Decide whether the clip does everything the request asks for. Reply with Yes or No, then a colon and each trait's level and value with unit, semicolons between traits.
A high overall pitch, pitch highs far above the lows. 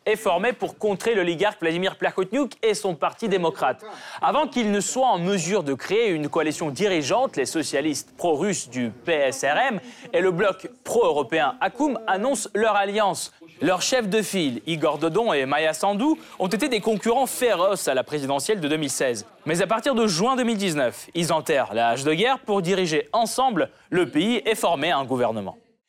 Yes: high, 200 Hz; wide, 6.3 semitones